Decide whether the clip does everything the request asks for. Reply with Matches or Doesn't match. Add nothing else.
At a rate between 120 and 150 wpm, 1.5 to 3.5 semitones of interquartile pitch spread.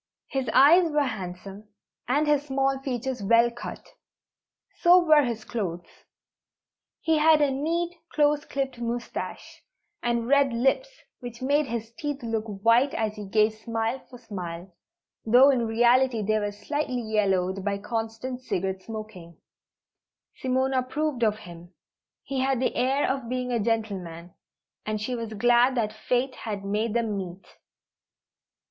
Doesn't match